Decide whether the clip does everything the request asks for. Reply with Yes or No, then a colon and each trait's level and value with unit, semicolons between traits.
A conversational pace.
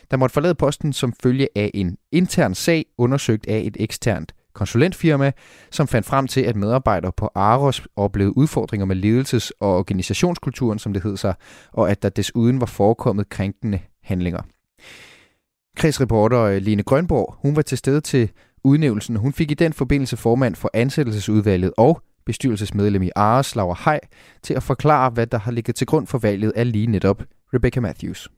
Yes: average, 170 wpm